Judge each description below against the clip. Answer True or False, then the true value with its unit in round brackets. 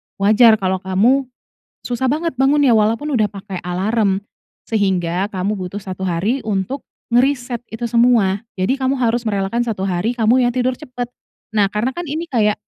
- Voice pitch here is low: False (225 Hz)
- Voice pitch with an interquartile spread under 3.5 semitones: False (4.3 semitones)